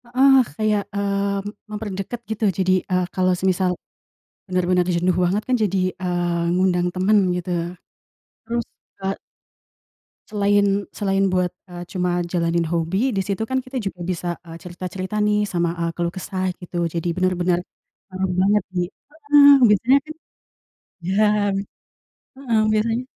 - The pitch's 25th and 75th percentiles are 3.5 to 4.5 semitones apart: No, average, 2.9 semitones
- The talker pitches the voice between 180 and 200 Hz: Yes, high, 190 Hz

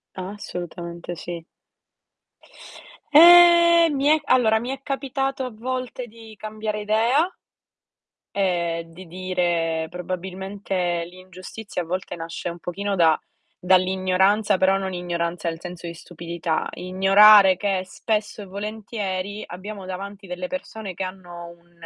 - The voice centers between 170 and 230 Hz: Yes, high, 190 Hz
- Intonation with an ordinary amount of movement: Yes, average, 3.5 semitones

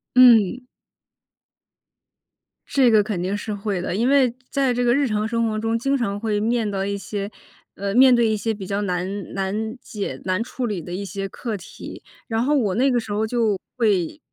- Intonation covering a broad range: No, average, 3.2 semitones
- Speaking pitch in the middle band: No, high, 215 Hz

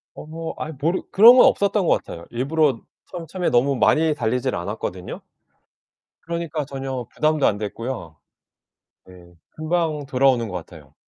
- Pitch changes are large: Yes, wide, 6.4 semitones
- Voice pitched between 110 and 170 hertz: Yes, low, 135 Hz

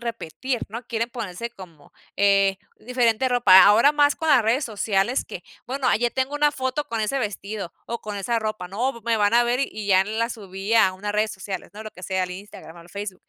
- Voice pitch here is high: Yes, high, 220 Hz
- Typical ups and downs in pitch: Yes, average, 3.6 semitones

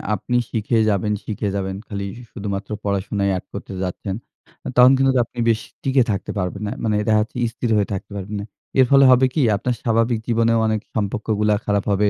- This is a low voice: Yes, low, 105 Hz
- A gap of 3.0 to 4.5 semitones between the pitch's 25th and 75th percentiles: No, narrow, 2.5 semitones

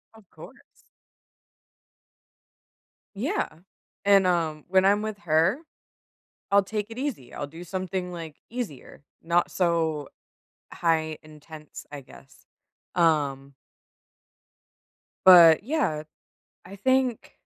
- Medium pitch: Yes, medium, 170 Hz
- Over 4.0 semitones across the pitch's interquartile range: Yes, average, 4.4 semitones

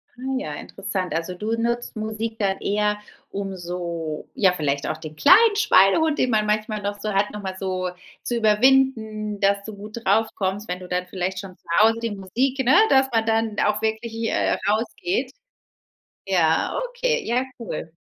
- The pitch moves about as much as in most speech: Yes, average, 3.3 semitones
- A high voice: Yes, high, 210 Hz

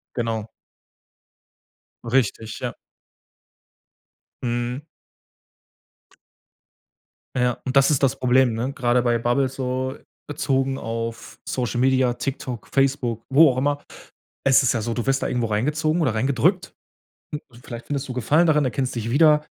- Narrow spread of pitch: Yes, narrow, 2.3 semitones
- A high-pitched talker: No, low, 130 Hz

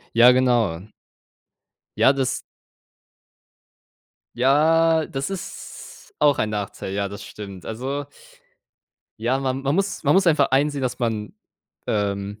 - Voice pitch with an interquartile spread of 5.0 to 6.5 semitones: Yes, average, 5.3 semitones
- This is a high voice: No, low, 130 Hz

